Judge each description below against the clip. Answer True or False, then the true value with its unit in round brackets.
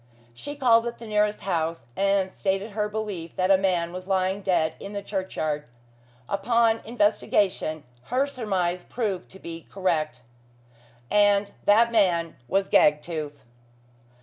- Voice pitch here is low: False (195 Hz)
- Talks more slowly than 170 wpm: True (135 wpm)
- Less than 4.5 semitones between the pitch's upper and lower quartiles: True (3.5 semitones)